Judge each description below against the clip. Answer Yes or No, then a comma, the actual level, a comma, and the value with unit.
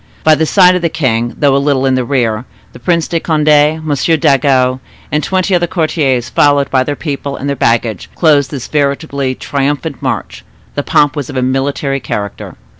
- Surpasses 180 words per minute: Yes, average, 190 wpm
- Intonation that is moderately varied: Yes, average, 3.0 semitones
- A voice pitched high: No, medium, 140 Hz